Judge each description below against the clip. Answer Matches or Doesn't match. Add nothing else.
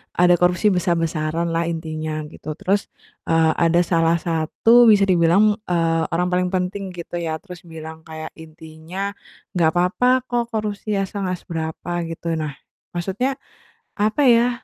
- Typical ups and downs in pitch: Matches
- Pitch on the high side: Doesn't match